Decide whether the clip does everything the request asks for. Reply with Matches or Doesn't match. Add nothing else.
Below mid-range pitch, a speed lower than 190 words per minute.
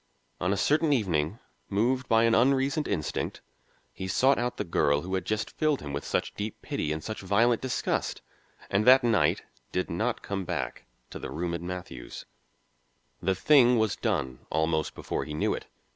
Matches